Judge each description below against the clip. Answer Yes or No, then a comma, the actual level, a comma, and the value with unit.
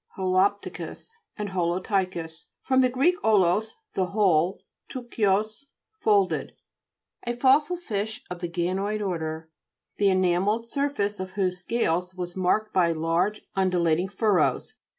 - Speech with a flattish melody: No, average, 3.3 semitones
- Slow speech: Yes, slow, 115 wpm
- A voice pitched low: No, high, 195 Hz